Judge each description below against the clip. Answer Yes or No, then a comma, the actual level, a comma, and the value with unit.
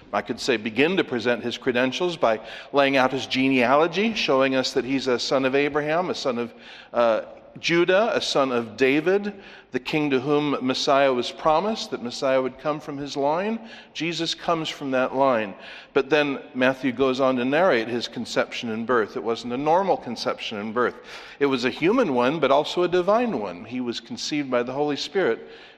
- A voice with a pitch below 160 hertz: Yes, medium, 140 Hz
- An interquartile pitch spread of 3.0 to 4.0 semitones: Yes, average, 3.6 semitones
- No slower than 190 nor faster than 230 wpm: Yes, average, 195 wpm